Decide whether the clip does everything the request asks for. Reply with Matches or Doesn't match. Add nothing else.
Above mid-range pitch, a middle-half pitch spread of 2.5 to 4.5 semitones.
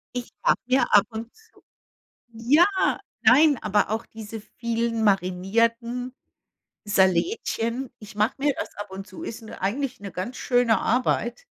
Matches